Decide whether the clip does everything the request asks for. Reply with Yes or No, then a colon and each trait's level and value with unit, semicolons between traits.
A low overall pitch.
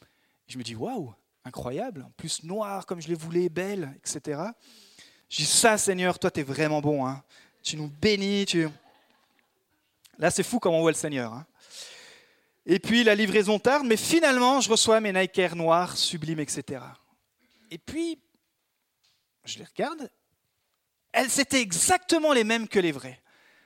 No: high, 195 Hz